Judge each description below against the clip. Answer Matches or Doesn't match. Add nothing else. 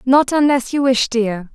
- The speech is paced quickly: Doesn't match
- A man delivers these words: Doesn't match